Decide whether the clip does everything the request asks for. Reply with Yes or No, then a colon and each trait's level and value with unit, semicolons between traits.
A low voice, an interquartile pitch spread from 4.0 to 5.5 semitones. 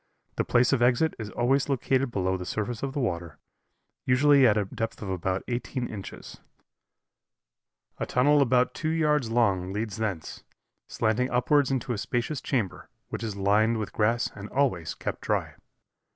Yes: low, 120 Hz; average, 4.3 semitones